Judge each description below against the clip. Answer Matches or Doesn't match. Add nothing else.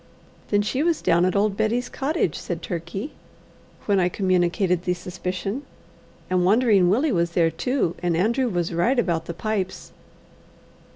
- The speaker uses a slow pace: Doesn't match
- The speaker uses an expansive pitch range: Doesn't match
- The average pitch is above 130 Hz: Matches